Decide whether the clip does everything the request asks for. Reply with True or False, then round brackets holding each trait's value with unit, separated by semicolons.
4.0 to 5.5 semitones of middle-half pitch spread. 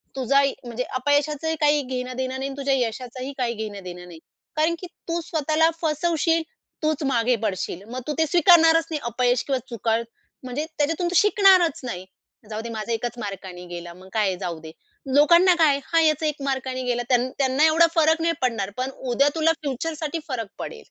True (5.1 semitones)